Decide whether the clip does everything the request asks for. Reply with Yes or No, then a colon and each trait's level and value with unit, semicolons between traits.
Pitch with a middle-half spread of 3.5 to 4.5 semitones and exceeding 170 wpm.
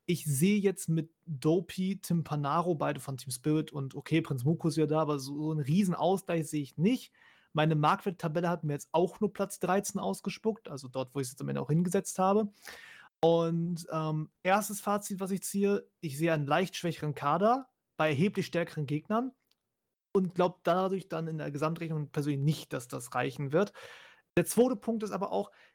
Yes: average, 4.2 semitones; fast, 190 wpm